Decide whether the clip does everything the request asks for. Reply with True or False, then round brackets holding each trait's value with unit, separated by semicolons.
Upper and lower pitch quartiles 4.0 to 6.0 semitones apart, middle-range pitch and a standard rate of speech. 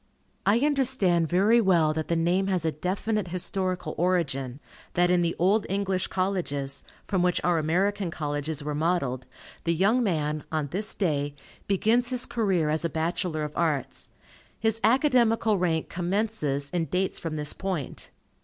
True (4.3 semitones; 175 Hz; 155 wpm)